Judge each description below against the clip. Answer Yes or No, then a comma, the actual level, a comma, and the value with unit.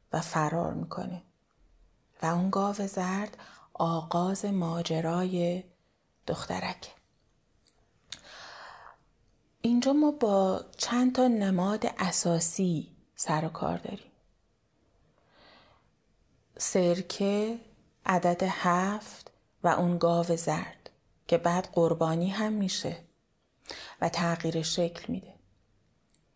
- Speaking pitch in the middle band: Yes, medium, 180 Hz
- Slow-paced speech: Yes, slow, 85 wpm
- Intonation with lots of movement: No, average, 2.9 semitones